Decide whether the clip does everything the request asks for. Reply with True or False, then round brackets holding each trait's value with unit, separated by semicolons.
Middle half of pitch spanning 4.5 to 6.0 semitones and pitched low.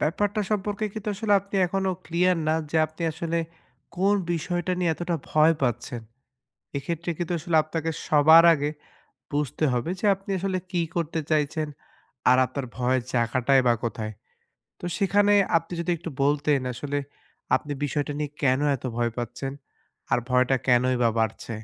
False (5.2 semitones; 155 Hz)